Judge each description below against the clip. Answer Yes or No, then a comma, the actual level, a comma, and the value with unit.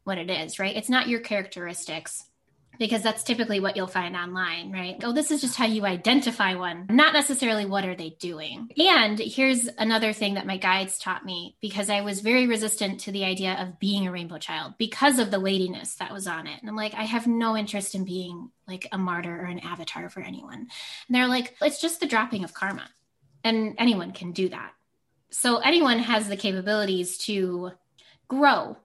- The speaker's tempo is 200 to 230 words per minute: Yes, fast, 205 wpm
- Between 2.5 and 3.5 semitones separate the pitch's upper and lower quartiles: No, average, 4.1 semitones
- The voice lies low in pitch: No, high, 205 Hz